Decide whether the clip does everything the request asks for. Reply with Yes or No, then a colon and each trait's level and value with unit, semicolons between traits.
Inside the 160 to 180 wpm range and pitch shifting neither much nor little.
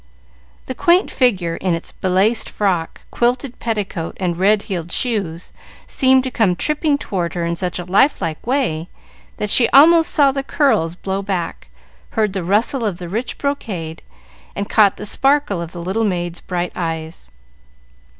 No: average, 165 wpm; wide, 6.2 semitones